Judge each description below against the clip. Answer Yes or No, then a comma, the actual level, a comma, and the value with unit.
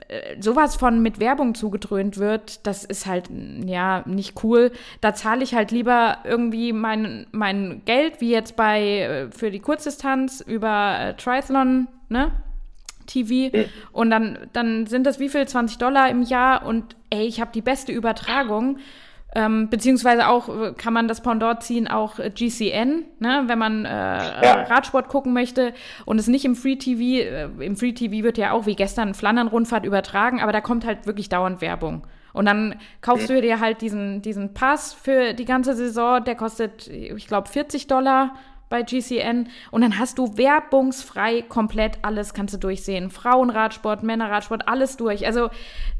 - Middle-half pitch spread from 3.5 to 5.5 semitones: No, average, 3.0 semitones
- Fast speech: No, average, 165 wpm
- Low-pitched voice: No, high, 230 Hz